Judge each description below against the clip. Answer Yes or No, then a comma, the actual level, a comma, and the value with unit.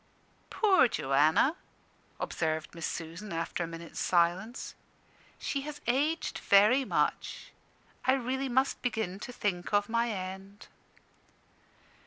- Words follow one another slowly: Yes, slow, 115 wpm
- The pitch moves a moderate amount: No, wide, 7.2 semitones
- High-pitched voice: Yes, high, 205 Hz